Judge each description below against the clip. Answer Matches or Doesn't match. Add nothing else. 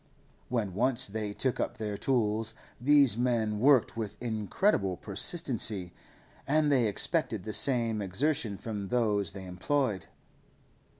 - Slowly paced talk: Matches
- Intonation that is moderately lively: Matches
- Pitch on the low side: Matches